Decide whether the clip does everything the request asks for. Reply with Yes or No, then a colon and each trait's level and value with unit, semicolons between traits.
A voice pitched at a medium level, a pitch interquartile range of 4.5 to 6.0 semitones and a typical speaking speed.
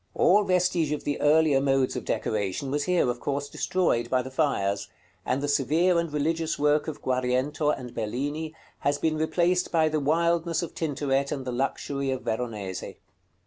No: medium, 145 Hz; average, 3.5 semitones; average, 175 wpm